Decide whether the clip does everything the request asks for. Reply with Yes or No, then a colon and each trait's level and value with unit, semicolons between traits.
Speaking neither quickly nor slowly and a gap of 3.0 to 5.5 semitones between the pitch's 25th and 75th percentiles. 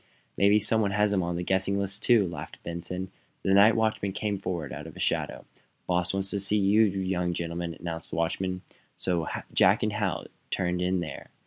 No: average, 195 wpm; narrow, 2.5 semitones